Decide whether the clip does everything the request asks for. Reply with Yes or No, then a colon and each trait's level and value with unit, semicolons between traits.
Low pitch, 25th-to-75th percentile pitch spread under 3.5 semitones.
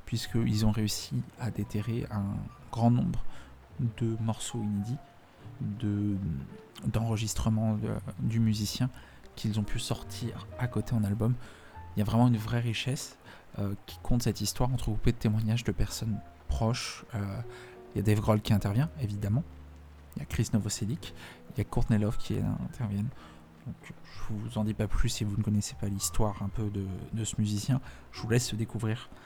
Yes: low, 110 Hz; narrow, 2.5 semitones